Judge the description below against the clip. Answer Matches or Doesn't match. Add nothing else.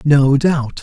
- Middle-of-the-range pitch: Matches